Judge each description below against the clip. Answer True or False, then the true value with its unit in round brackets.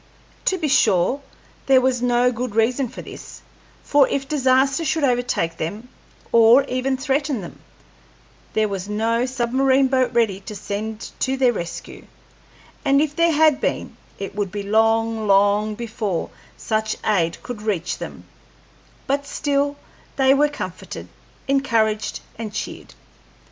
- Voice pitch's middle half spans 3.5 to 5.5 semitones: True (4.2 semitones)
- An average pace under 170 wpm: True (140 wpm)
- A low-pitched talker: False (240 Hz)